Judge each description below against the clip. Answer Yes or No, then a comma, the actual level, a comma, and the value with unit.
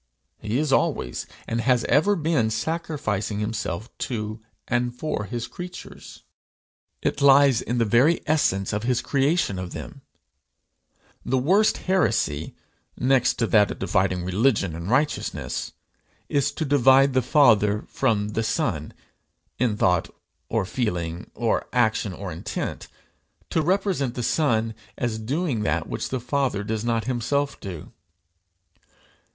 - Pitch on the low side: Yes, low, 120 Hz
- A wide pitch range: No, average, 4.9 semitones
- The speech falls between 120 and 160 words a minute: Yes, slow, 135 wpm